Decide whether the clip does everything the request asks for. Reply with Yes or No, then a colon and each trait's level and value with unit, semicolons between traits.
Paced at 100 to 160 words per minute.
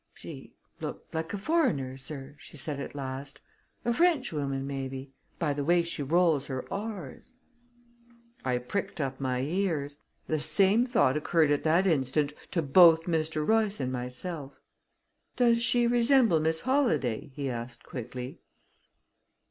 Yes: average, 140 wpm